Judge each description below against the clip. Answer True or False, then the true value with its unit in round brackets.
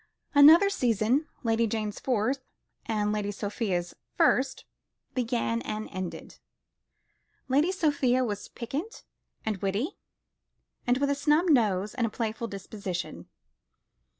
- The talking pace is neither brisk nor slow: False (110 wpm)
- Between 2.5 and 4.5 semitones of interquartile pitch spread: False (4.9 semitones)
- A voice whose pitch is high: True (230 Hz)